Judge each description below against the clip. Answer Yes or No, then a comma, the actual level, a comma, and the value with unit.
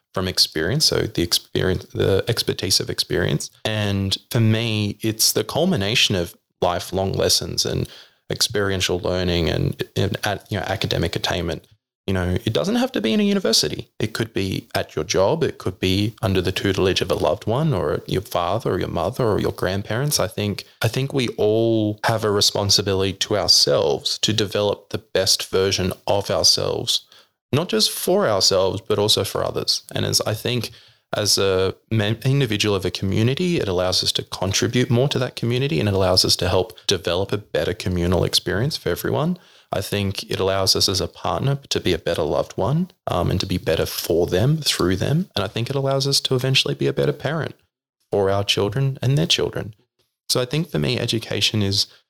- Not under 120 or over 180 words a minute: No, average, 195 wpm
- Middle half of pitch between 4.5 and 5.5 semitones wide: Yes, average, 4.9 semitones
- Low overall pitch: Yes, low, 110 Hz